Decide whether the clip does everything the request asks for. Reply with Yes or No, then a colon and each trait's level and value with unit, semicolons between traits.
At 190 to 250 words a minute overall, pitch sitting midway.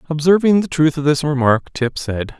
Yes: average, 200 wpm; medium, 150 Hz